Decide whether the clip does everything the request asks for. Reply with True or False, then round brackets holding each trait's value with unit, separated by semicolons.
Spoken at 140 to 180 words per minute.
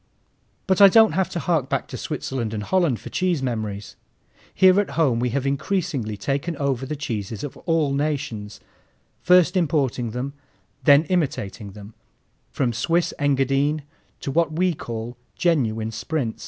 True (155 wpm)